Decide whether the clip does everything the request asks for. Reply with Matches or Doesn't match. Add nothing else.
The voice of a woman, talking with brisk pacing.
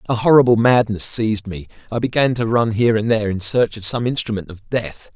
Doesn't match